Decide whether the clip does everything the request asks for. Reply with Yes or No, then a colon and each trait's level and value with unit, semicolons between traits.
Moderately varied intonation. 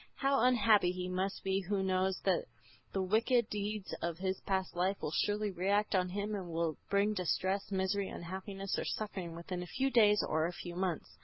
No: narrow, 2.2 semitones